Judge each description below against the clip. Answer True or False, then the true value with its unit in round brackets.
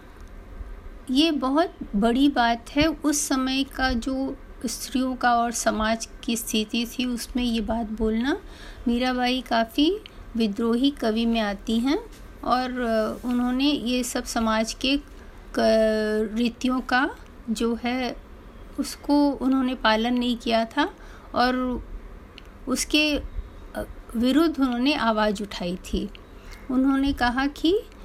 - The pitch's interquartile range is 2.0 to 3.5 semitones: True (3.1 semitones)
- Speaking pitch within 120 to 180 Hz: False (245 Hz)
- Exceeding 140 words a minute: False (115 wpm)